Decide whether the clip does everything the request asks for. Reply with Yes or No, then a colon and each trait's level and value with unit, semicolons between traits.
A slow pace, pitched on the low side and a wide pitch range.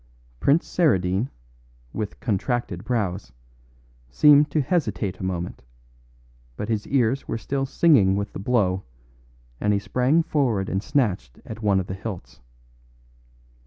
Yes: slow, 130 wpm; low, 110 Hz; wide, 6.1 semitones